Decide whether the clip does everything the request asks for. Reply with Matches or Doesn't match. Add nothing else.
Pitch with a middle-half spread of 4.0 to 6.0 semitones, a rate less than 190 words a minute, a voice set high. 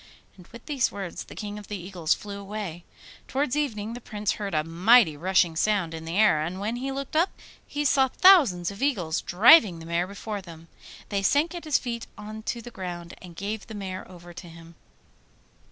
Doesn't match